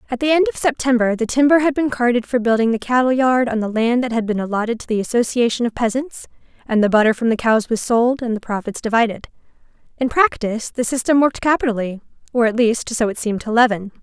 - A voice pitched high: Yes, high, 235 Hz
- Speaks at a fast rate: Yes, fast, 220 wpm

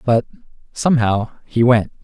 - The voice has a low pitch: Yes, low, 115 Hz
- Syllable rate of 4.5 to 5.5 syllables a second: Yes, 4.8 syllables/s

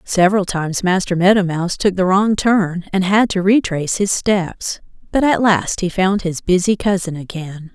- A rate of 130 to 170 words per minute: No, average, 185 wpm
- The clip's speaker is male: No, female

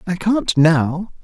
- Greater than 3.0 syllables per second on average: No, 2.9 syllables/s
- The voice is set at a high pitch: No, medium, 175 Hz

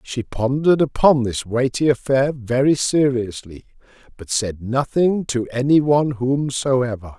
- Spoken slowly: Yes, slow, 125 wpm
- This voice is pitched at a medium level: No, low, 130 Hz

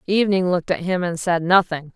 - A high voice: No, medium, 180 Hz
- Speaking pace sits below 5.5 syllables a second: No, 6.1 syllables/s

